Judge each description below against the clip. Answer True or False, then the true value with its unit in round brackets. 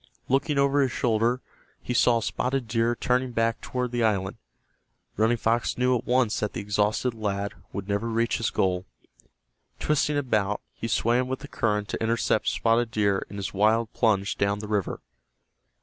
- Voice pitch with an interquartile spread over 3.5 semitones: False (3.0 semitones)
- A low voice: True (115 Hz)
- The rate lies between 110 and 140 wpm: False (170 wpm)